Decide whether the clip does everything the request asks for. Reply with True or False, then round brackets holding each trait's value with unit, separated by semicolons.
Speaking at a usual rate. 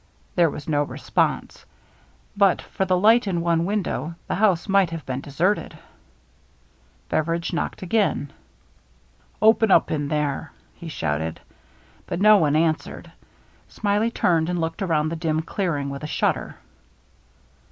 True (150 wpm)